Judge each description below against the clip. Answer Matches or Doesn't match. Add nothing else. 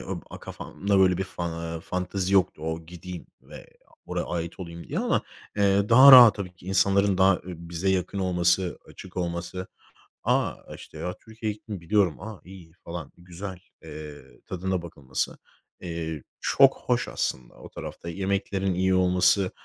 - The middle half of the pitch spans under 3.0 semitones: Matches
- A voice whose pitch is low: Matches